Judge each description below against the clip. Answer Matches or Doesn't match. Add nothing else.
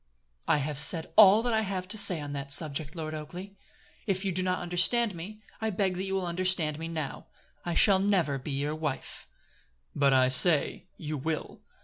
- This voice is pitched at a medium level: Matches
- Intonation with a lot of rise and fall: Doesn't match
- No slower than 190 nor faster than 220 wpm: Matches